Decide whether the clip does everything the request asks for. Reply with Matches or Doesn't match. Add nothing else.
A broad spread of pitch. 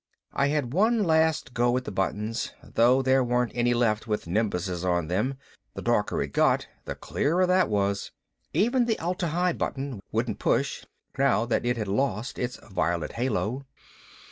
Matches